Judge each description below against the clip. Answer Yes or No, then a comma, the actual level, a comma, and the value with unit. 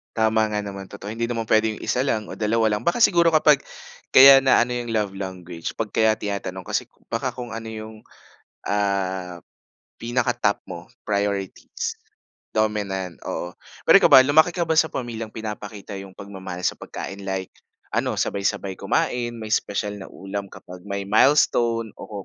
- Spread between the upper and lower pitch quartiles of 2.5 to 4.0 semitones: Yes, average, 3.1 semitones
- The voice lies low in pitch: Yes, low, 105 Hz